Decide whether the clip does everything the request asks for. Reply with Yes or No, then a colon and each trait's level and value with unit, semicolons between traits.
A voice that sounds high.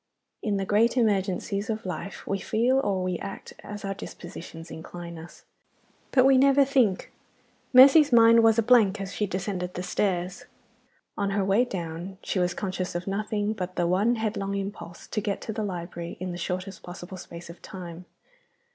Yes: high, 195 Hz